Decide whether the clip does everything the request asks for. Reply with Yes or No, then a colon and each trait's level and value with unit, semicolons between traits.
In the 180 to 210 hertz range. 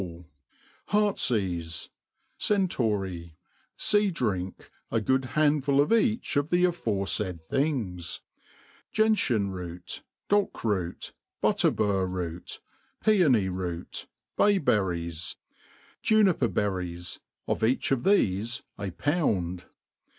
No: low, 105 Hz